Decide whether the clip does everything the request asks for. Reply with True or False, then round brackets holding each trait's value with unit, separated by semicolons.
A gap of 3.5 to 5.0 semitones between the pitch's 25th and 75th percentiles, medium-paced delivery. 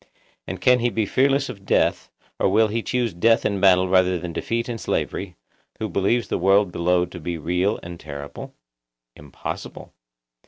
True (4.4 semitones; 170 wpm)